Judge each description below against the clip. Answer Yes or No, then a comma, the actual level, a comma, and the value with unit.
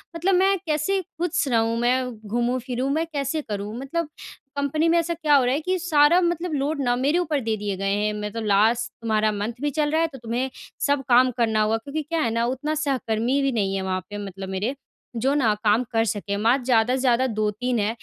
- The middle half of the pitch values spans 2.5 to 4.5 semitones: No, average, 5.2 semitones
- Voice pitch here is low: No, very high, 250 Hz